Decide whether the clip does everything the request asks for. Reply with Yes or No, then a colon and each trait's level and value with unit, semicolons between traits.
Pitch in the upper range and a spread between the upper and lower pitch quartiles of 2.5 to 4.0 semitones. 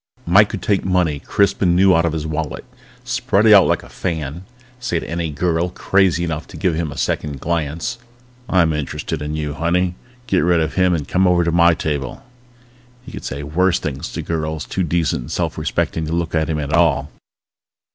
No: very low, 85 Hz; average, 2.8 semitones